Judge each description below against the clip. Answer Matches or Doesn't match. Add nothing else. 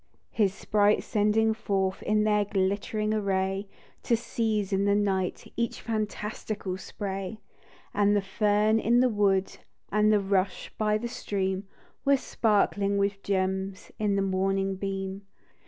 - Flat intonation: Matches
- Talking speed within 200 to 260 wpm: Doesn't match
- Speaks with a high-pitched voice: Matches